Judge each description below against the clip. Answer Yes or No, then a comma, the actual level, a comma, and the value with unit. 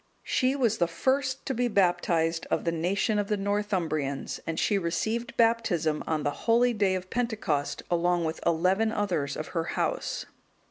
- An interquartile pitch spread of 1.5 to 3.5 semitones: No, wide, 5.4 semitones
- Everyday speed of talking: Yes, average, 170 wpm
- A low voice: No, medium, 185 Hz